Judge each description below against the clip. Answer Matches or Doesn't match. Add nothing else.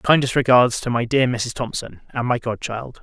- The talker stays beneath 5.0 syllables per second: Matches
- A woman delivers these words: Doesn't match